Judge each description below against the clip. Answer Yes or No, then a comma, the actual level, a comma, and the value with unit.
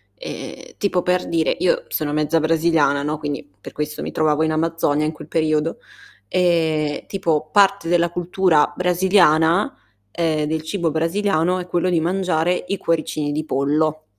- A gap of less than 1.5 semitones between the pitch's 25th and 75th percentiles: No, narrow, 2.6 semitones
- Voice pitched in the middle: Yes, medium, 165 Hz